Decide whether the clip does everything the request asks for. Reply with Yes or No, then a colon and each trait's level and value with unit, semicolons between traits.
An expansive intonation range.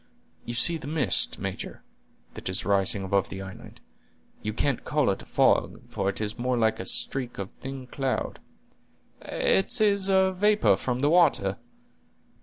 Yes: wide, 7.8 semitones